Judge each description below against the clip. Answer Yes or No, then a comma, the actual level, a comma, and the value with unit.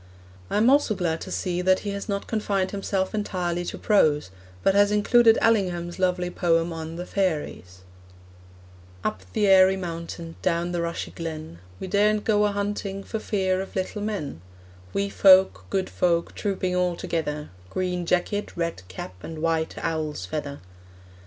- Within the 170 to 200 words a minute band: No, average, 160 wpm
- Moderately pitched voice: Yes, medium, 180 Hz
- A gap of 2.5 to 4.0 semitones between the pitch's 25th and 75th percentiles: Yes, average, 3.2 semitones